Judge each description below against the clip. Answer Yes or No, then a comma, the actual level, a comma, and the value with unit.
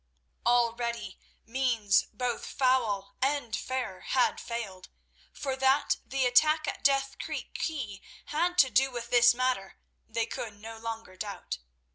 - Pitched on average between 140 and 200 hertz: No, high, 245 Hz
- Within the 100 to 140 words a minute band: Yes, slow, 135 wpm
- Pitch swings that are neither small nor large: Yes, average, 3.0 semitones